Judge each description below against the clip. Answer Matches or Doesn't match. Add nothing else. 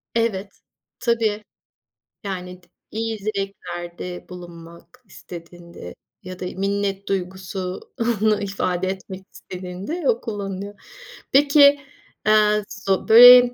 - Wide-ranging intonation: Doesn't match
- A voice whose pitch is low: Doesn't match